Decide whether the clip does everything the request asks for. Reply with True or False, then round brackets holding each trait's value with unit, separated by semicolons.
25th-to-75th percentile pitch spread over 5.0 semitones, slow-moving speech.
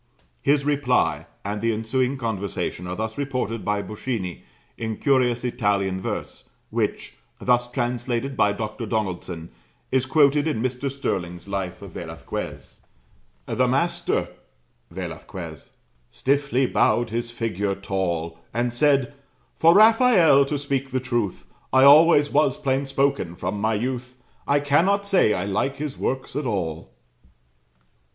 True (5.6 semitones; 130 wpm)